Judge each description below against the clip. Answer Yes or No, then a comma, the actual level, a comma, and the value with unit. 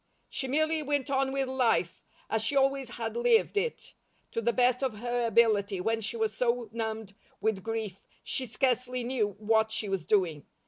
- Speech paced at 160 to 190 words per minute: Yes, average, 180 wpm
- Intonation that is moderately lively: Yes, average, 3.0 semitones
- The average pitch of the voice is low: No, high, 230 Hz